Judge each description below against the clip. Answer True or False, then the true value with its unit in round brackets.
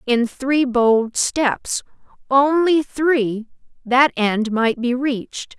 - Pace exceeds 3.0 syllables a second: False (2.9 syllables/s)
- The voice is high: True (255 Hz)